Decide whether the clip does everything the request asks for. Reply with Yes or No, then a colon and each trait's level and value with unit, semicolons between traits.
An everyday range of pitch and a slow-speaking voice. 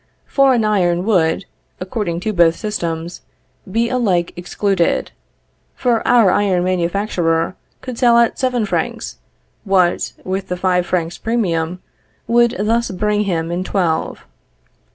Yes: average, 4.4 semitones; slow, 125 wpm